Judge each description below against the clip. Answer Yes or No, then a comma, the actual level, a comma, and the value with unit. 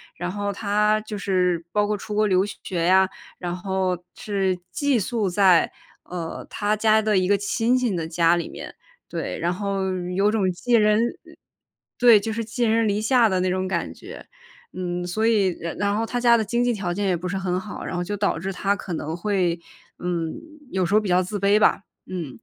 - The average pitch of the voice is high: Yes, high, 195 Hz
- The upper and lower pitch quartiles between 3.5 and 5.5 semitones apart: No, average, 2.9 semitones